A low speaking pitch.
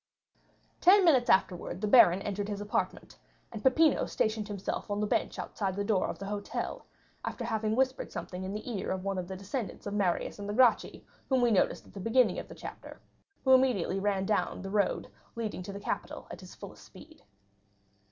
No: high, 205 Hz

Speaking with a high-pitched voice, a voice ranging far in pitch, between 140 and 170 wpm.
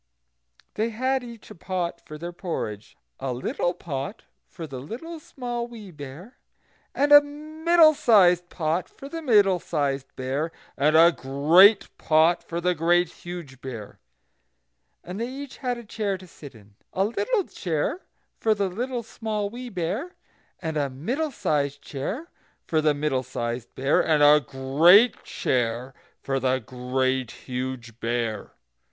No: medium, 170 Hz; wide, 9.0 semitones; average, 150 wpm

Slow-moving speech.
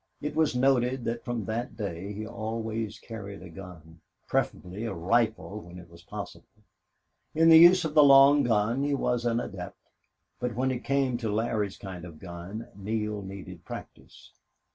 No: average, 175 wpm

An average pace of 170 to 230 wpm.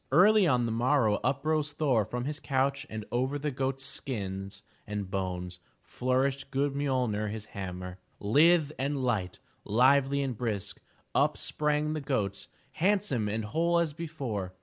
No: average, 150 wpm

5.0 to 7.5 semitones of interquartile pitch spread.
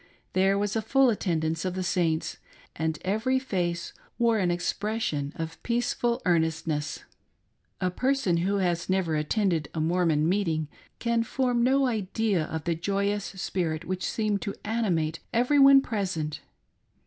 Yes: average, 5.3 semitones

